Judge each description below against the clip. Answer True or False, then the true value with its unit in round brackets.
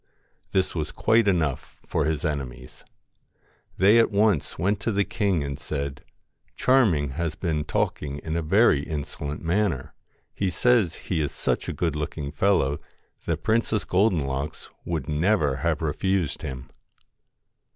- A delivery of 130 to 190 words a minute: True (150 wpm)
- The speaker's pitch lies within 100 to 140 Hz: False (80 Hz)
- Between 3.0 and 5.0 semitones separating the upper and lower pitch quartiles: False (5.4 semitones)